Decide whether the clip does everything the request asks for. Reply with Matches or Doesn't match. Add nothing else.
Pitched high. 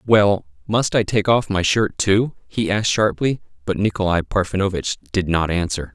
Doesn't match